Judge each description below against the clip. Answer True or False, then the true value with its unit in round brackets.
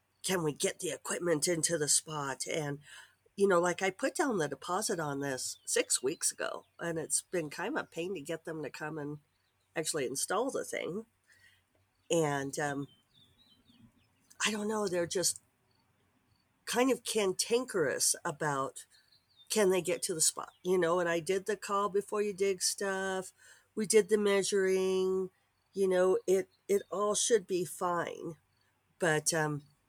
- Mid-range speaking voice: True (175 Hz)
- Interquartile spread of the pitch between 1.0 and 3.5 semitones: False (5.1 semitones)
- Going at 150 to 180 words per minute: True (165 wpm)